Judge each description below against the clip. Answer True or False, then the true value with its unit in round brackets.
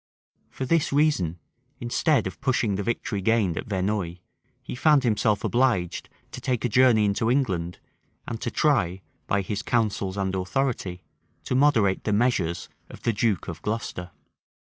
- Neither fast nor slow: True (160 wpm)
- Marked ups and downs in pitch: False (4.8 semitones)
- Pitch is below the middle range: True (105 Hz)